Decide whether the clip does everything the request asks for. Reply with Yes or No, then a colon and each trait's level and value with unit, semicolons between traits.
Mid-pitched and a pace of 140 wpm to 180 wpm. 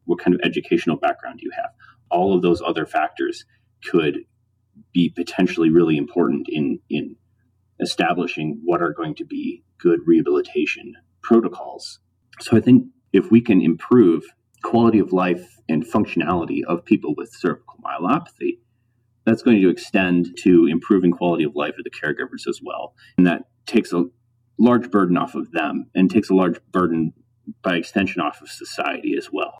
No: low, 120 Hz; average, 165 wpm